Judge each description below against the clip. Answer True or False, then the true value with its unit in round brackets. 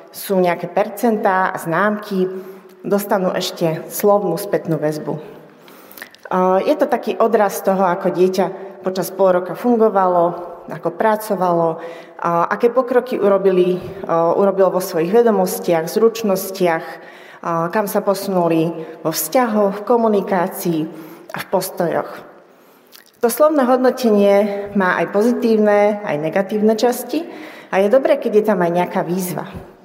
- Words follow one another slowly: False (120 wpm)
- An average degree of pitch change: True (3.5 semitones)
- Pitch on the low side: False (190 Hz)